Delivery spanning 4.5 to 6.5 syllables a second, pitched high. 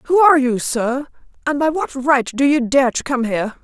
Yes: 5.0 syllables/s; very high, 265 Hz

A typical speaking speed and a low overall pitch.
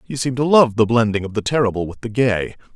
No: fast, 260 wpm; low, 115 Hz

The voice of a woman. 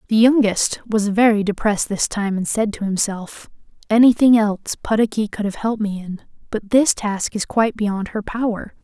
Yes: female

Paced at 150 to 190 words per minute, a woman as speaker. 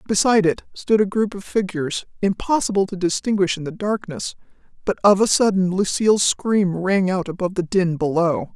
Yes: average, 175 wpm; female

